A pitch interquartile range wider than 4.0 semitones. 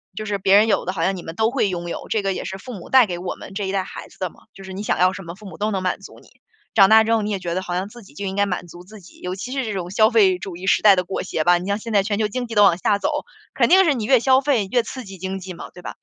No: average, 3.0 semitones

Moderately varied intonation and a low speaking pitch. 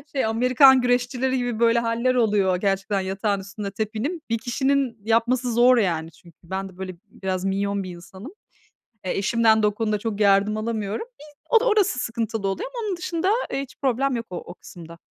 No: average, 4.4 semitones; high, 225 Hz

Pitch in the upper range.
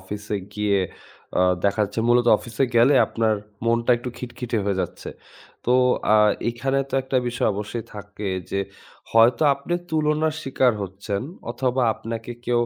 No: low, 115 Hz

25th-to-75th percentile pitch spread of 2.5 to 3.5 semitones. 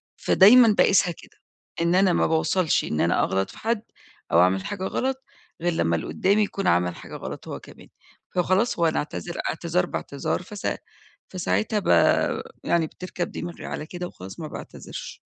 No: average, 4.3 semitones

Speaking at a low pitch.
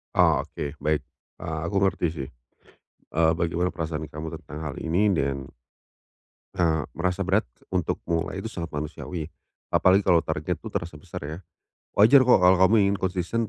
Yes: very low, 85 Hz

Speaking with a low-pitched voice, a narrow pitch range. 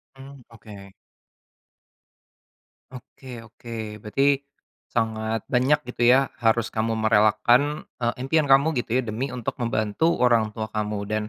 No: low, 115 Hz; average, 3.4 semitones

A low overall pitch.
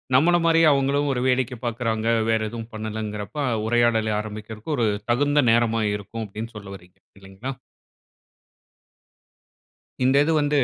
Yes: low, 115 Hz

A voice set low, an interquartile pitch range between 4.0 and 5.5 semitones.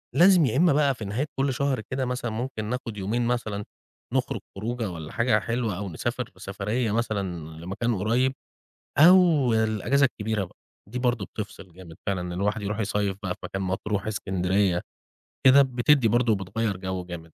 Yes: low, 110 Hz; average, 4.3 semitones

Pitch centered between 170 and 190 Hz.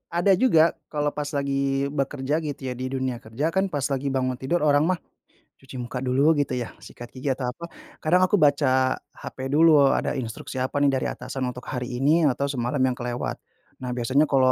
No: low, 135 Hz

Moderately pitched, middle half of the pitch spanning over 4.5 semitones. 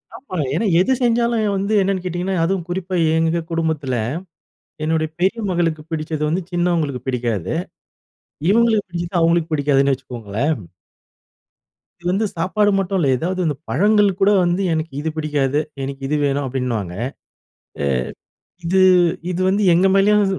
Yes: medium, 170 Hz; average, 4.9 semitones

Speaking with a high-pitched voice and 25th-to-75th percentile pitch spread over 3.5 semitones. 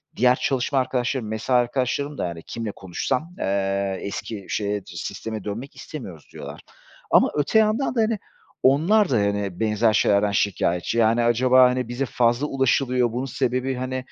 No: low, 120 Hz; average, 4.2 semitones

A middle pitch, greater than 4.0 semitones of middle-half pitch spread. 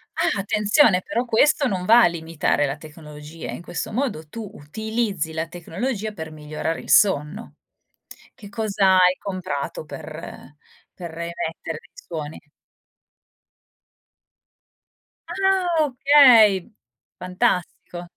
Yes: medium, 180 Hz; wide, 5.6 semitones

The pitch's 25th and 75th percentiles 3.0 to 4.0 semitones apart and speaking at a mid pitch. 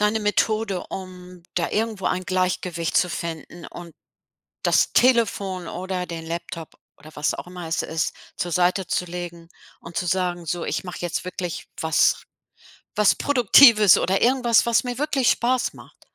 Yes: average, 3.7 semitones; medium, 180 Hz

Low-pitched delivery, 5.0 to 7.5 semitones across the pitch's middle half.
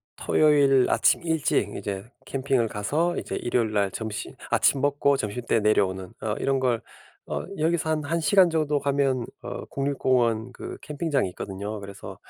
Yes: low, 130 Hz; average, 5.3 semitones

